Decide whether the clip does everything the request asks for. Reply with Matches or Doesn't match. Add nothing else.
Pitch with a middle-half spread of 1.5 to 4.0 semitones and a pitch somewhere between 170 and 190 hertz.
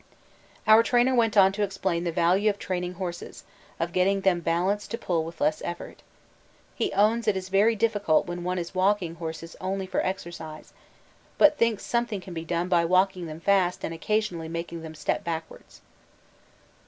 Matches